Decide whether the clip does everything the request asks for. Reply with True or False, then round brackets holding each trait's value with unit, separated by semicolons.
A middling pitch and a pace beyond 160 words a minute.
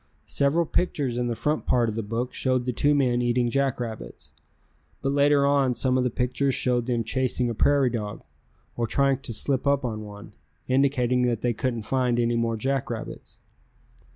False (125 Hz; 180 wpm)